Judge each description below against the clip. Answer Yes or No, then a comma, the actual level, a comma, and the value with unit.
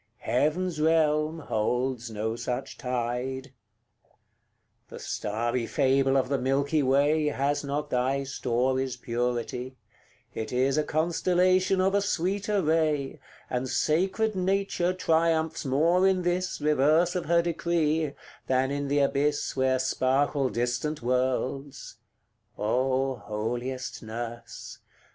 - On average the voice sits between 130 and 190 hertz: Yes, medium, 140 Hz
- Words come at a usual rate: No, slow, 115 wpm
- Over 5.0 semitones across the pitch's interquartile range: No, average, 4.2 semitones